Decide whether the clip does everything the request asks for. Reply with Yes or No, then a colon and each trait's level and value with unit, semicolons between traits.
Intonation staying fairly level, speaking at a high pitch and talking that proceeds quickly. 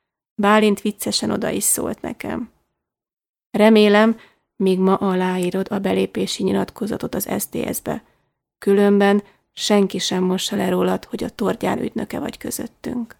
No: narrow, 2.1 semitones; high, 195 Hz; average, 125 wpm